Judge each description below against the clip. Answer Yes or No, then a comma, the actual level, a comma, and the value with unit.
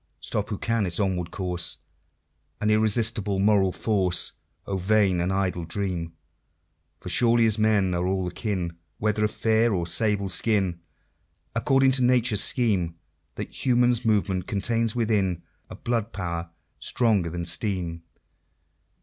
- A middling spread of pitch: Yes, average, 3.7 semitones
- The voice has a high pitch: No, low, 100 Hz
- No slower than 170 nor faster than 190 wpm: No, slow, 135 wpm